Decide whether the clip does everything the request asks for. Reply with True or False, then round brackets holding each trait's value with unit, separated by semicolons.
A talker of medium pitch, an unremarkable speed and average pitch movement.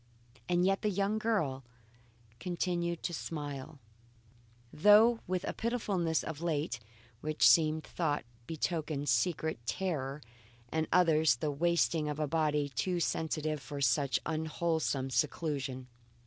False (160 Hz; 120 wpm; 3.1 semitones)